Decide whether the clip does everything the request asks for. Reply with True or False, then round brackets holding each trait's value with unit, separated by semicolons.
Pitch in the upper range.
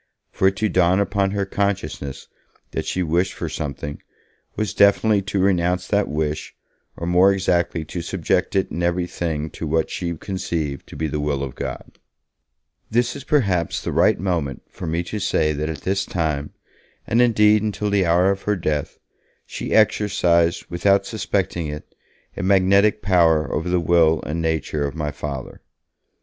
False (90 Hz)